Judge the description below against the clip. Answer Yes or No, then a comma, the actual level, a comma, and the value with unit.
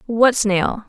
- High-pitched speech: Yes, high, 215 Hz